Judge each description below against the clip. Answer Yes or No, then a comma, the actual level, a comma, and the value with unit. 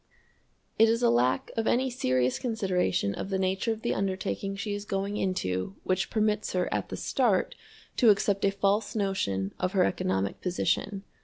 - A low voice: No, high, 195 Hz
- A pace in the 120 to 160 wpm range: No, average, 175 wpm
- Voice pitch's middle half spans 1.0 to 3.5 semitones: Yes, average, 2.9 semitones